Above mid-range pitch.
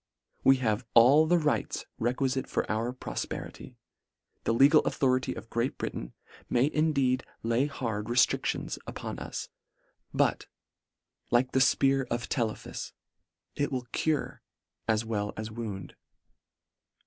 No: low, 125 Hz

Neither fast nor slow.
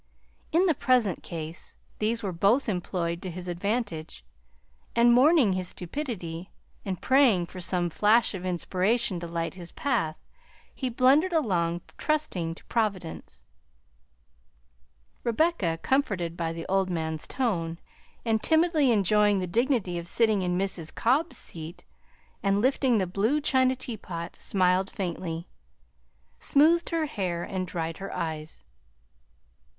No: slow, 130 wpm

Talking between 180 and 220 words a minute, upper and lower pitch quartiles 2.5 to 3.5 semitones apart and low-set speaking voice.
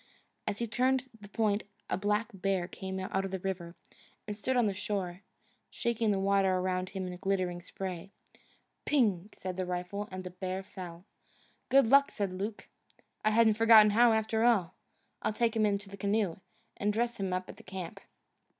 No: average, 185 wpm; average, 2.9 semitones; high, 200 Hz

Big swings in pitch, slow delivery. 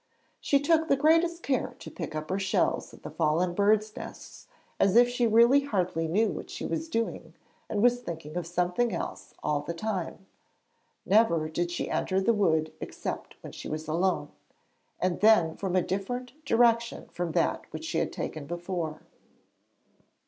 No: wide, 5.7 semitones; average, 165 wpm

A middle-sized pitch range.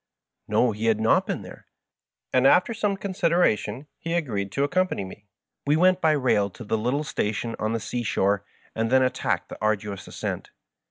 No: wide, 7.0 semitones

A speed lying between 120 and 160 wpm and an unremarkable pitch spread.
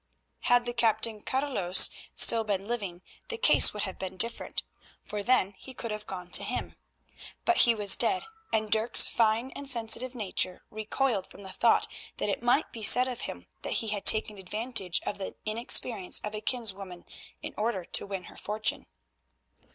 No: average, 180 wpm; average, 3.4 semitones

